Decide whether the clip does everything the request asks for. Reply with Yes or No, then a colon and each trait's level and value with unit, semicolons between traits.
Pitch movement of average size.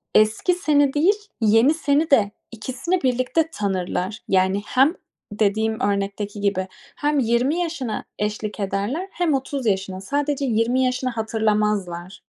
No: wide, 5.7 semitones